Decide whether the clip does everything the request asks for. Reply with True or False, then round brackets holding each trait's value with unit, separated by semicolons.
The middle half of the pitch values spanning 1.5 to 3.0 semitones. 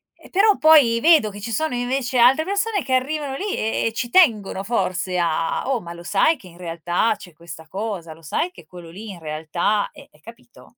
False (7.7 semitones)